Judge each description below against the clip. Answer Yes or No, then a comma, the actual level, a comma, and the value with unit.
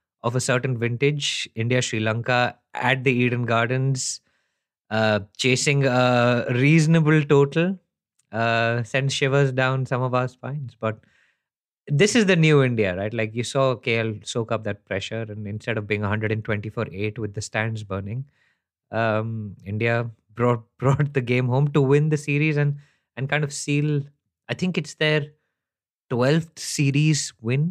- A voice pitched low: Yes, low, 125 Hz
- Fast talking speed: No, average, 155 wpm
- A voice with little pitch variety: No, average, 4.2 semitones